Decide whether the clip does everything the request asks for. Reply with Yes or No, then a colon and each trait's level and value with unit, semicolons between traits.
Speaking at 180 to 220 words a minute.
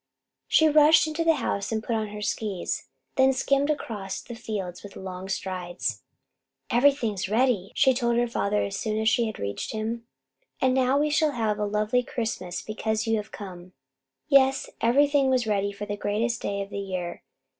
Yes: average, 185 wpm